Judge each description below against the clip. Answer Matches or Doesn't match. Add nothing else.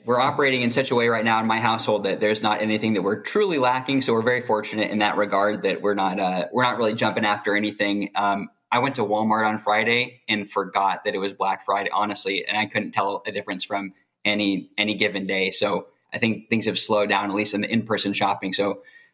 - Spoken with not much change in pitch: Matches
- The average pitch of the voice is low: Matches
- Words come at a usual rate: Doesn't match